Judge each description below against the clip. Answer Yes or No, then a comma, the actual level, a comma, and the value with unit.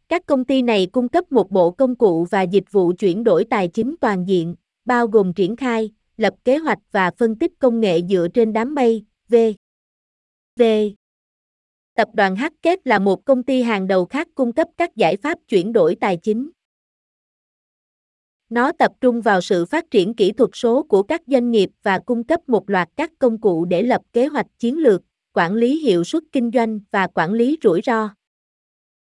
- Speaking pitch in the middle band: No, high, 230 Hz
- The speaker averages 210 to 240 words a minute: No, average, 195 wpm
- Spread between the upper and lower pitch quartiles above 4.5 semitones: Yes, average, 5.3 semitones